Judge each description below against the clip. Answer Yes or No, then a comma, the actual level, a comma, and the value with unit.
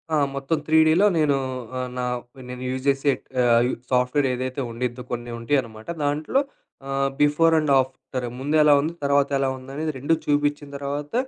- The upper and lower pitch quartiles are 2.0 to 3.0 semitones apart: Yes, narrow, 2.5 semitones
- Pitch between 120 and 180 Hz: Yes, medium, 140 Hz